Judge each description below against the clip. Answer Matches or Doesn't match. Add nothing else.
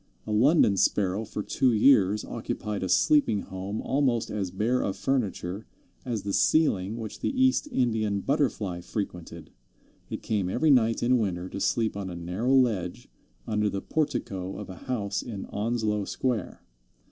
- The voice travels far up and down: Doesn't match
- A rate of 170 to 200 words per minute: Doesn't match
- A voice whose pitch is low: Matches